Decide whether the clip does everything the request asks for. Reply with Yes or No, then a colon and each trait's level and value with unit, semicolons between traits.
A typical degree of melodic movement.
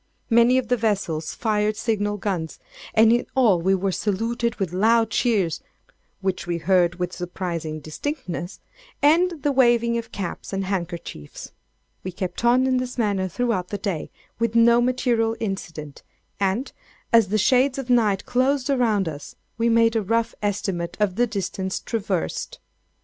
Yes: average, 4.3 semitones